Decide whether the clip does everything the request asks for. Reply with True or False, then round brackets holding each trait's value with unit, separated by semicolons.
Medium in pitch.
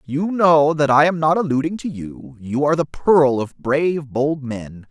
True (145 Hz)